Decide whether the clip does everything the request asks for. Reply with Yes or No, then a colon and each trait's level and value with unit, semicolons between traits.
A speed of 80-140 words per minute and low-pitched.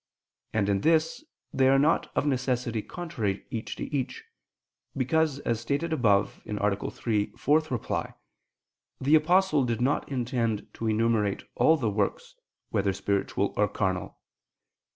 Yes: slow, 135 wpm; low, 120 Hz